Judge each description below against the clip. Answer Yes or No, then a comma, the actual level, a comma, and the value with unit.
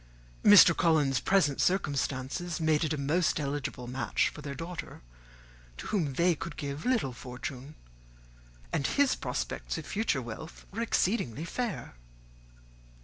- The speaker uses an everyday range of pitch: Yes, average, 4.7 semitones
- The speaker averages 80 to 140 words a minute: Yes, slow, 135 wpm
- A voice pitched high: No, medium, 155 Hz